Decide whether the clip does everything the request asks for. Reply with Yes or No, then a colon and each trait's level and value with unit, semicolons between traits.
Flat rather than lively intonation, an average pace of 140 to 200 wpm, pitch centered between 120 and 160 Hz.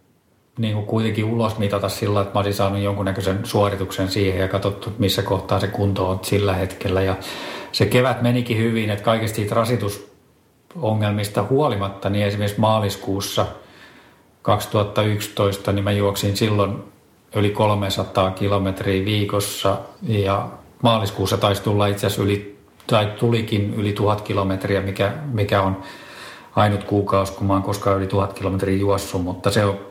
No: narrow, 1.5 semitones; average, 145 wpm; low, 100 Hz